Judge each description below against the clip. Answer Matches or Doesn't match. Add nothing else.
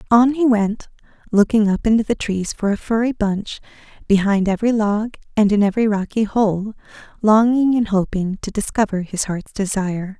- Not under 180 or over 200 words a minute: Doesn't match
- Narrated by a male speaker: Doesn't match